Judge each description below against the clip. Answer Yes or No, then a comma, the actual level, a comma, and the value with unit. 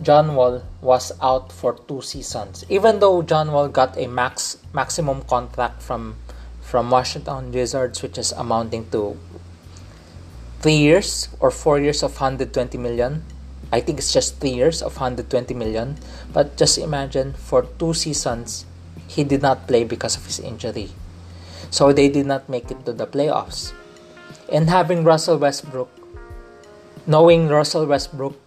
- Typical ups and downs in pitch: No, wide, 7.1 semitones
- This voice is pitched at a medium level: No, low, 130 Hz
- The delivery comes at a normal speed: Yes, average, 150 wpm